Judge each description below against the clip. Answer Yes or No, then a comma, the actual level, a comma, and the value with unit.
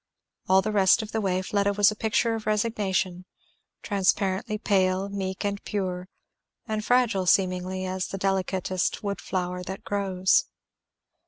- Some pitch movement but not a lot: No, narrow, 2.0 semitones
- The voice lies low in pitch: No, high, 195 Hz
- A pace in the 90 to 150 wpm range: Yes, average, 145 wpm